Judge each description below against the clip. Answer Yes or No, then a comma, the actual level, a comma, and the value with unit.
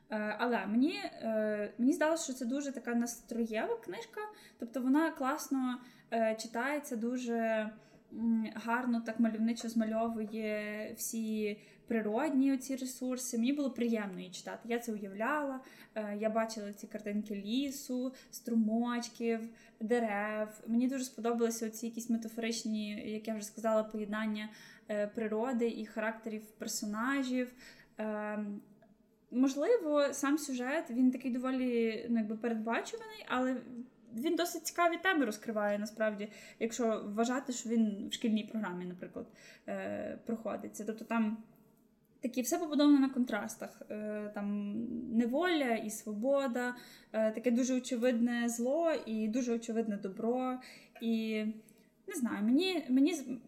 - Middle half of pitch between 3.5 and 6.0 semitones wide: No, average, 2.7 semitones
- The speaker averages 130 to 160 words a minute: No, average, 115 wpm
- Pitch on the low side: No, high, 230 Hz